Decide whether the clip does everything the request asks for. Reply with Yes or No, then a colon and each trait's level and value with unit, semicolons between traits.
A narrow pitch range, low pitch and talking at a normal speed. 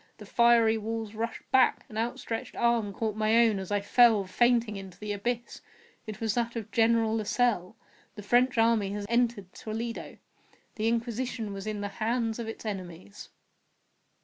No: narrow, 2.2 semitones; high, 225 Hz; average, 165 wpm